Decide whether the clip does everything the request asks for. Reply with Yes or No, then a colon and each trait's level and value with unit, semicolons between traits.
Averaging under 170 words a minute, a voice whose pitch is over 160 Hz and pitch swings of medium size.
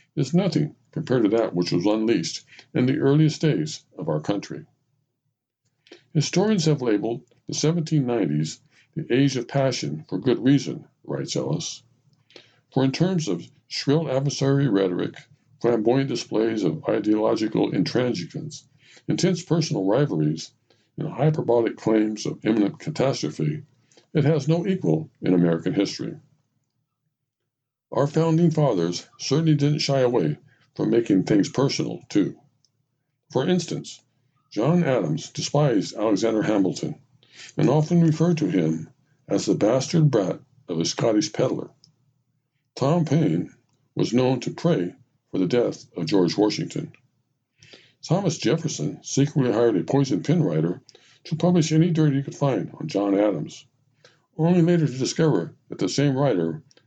No: slow, 135 wpm; medium, 140 Hz; average, 4.4 semitones